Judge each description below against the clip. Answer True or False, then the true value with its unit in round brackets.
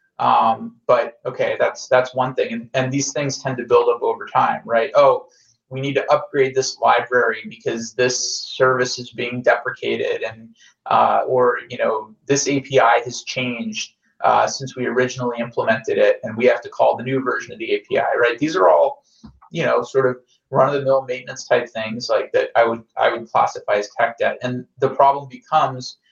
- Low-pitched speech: True (130 Hz)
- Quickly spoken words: False (190 wpm)